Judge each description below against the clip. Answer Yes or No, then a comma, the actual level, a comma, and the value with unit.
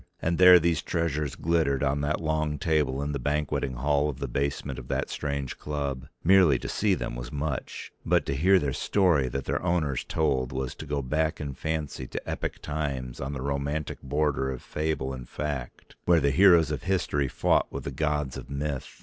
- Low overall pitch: Yes, very low, 75 Hz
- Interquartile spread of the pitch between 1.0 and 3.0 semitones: Yes, narrow, 2.5 semitones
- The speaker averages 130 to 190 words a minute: No, average, 200 wpm